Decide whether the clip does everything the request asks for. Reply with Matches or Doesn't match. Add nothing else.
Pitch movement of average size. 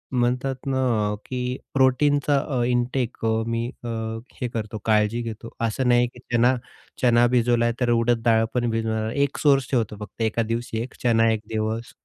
Doesn't match